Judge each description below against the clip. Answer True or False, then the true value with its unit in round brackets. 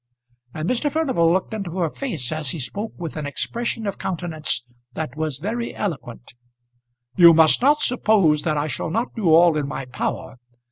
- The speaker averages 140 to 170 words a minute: False (180 wpm)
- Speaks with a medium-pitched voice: True (165 Hz)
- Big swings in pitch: True (6.1 semitones)